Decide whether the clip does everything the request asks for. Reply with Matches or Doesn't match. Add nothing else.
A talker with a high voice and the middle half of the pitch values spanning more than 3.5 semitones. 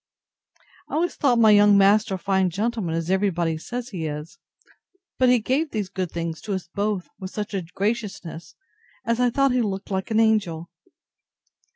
Matches